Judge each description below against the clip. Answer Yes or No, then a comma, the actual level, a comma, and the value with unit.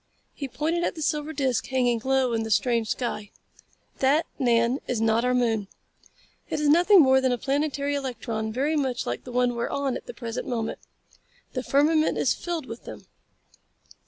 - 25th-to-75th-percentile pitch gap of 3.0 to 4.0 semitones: Yes, average, 3.6 semitones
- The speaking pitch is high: Yes, very high, 260 Hz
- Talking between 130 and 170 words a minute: No, average, 190 wpm